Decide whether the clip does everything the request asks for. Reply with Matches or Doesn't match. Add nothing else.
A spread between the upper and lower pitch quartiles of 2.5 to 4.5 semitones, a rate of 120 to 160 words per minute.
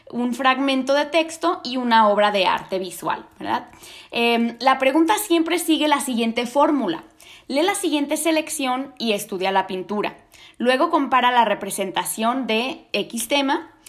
Doesn't match